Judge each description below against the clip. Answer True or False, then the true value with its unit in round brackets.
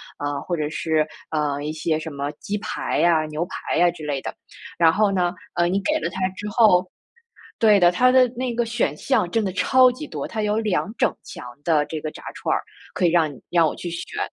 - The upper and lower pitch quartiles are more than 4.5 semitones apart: True (5.2 semitones)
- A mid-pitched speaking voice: True (175 Hz)